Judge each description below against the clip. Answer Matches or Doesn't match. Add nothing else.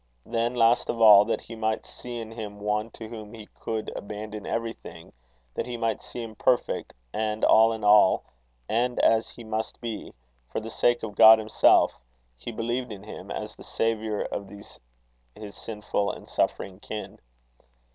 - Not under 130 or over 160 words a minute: Doesn't match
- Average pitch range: Doesn't match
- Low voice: Matches